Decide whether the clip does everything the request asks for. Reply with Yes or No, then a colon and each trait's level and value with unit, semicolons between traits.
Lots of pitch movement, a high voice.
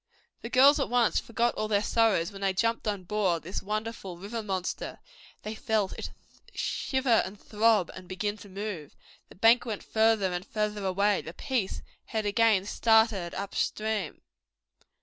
No: average, 2.8 semitones; high, 210 Hz